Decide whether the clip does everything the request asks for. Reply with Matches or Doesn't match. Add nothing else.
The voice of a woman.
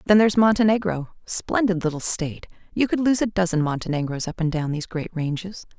Matches